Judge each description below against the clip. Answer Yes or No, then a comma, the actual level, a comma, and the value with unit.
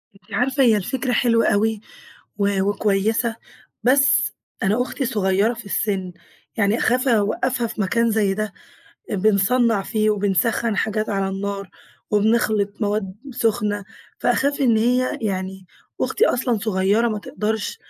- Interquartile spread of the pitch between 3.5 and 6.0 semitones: No, average, 2.7 semitones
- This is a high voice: Yes, high, 215 Hz